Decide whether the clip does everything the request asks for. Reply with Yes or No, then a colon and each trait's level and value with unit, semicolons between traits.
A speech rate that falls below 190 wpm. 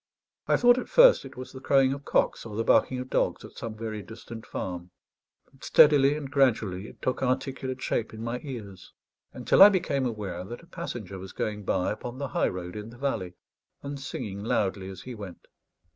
No: fast, 205 wpm